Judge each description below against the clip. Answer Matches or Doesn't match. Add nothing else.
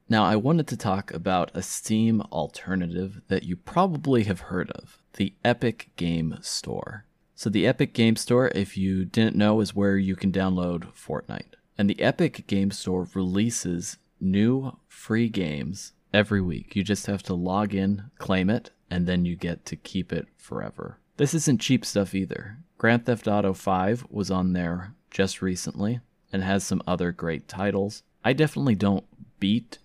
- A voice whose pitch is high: Doesn't match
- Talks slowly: Doesn't match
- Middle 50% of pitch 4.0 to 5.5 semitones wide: Doesn't match